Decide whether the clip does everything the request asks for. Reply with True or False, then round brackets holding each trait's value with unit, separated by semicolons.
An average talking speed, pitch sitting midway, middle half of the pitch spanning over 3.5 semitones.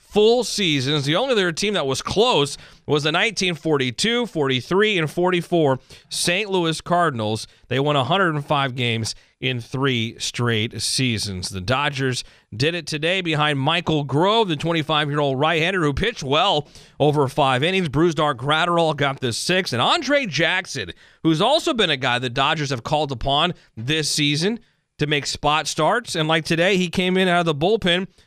True (165 wpm; 155 Hz; 4.4 semitones)